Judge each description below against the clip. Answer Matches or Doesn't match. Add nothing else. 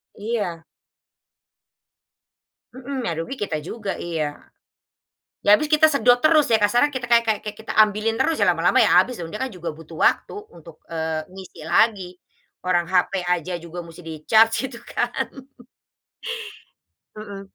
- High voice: Matches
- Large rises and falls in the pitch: Matches